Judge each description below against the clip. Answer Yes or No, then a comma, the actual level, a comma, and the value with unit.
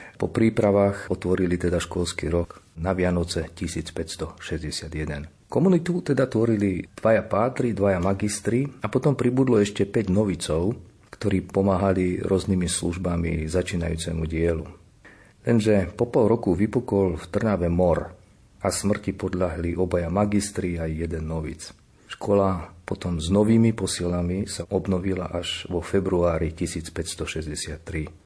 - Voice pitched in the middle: No, very low, 90 Hz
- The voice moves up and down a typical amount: Yes, average, 3.1 semitones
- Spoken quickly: No, average, 115 wpm